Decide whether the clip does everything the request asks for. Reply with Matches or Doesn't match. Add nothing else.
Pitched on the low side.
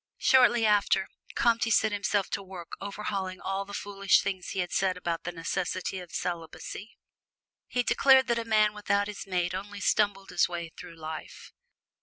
Doesn't match